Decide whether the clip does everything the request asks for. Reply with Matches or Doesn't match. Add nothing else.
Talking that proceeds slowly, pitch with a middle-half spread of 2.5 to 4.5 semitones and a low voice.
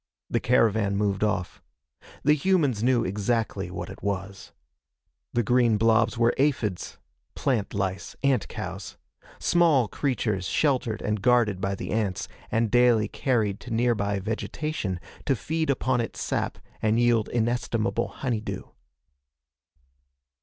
Matches